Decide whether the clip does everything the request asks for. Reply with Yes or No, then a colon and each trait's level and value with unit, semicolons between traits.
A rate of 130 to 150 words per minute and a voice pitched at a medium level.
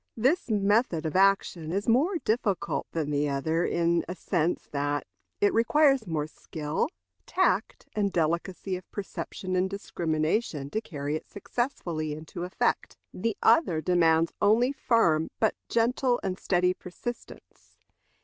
Yes: slow, 135 wpm; medium, 180 Hz